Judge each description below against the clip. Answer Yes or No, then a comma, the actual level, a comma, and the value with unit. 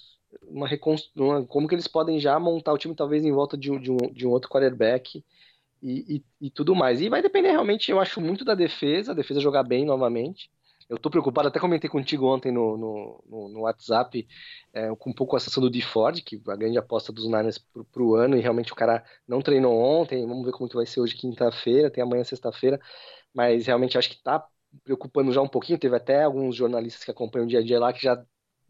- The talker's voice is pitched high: No, low, 130 Hz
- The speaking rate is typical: No, fast, 230 wpm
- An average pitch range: Yes, average, 3.4 semitones